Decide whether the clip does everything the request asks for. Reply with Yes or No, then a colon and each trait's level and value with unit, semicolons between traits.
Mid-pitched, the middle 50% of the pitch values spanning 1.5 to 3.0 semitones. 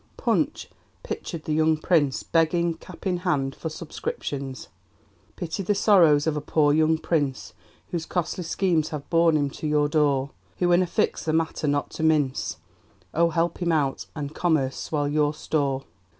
Yes: medium, 155 Hz; narrow, 2.5 semitones